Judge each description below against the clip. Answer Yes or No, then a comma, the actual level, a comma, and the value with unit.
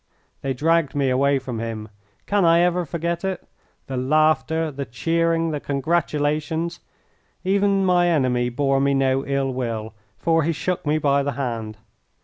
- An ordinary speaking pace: Yes, average, 155 wpm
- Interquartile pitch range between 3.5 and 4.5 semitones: Yes, average, 4.0 semitones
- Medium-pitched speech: Yes, medium, 145 Hz